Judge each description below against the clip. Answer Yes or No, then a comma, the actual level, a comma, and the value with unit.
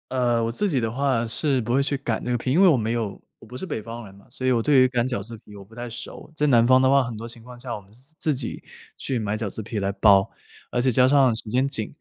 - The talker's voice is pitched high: No, low, 120 Hz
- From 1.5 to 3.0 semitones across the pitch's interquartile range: Yes, average, 2.7 semitones